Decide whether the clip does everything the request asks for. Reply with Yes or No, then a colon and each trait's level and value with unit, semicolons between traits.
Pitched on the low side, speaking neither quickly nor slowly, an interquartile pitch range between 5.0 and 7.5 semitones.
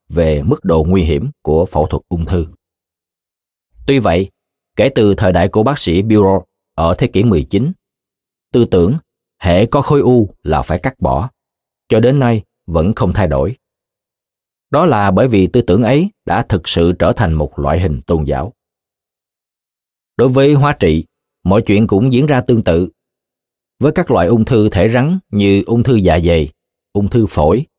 Yes: very low, 95 Hz; average, 180 wpm; wide, 5.5 semitones